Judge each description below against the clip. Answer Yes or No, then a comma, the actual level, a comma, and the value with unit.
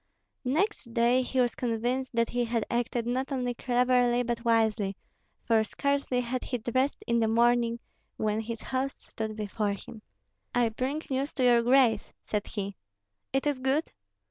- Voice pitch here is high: Yes, high, 240 Hz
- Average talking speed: Yes, average, 165 wpm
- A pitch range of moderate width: No, narrow, 2.2 semitones